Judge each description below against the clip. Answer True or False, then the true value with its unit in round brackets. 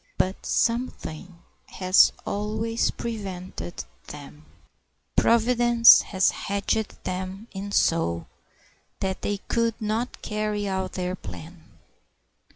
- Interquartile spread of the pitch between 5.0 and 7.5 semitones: False (3.4 semitones)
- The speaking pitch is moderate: False (200 Hz)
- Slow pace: True (95 wpm)